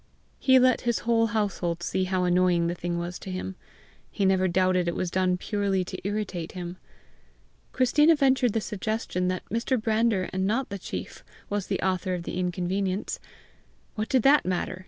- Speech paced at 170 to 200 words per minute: Yes, average, 180 wpm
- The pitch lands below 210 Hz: Yes, high, 190 Hz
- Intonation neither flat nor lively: Yes, average, 3.6 semitones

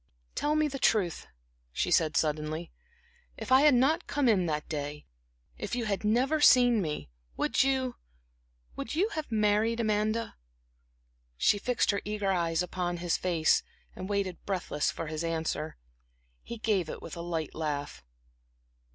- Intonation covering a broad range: Yes, wide, 6.6 semitones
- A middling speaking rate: Yes, average, 155 wpm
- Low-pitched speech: No, high, 200 Hz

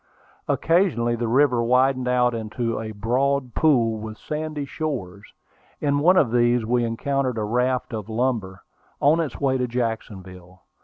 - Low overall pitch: Yes, low, 125 Hz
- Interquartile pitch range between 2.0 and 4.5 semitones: Yes, average, 3.6 semitones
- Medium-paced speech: Yes, average, 150 wpm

